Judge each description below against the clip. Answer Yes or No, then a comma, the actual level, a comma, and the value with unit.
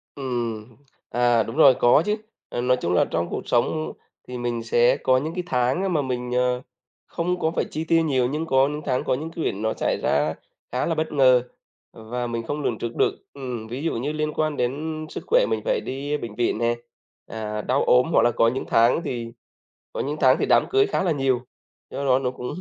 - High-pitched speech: No, low, 130 Hz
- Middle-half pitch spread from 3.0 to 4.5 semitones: Yes, average, 4.2 semitones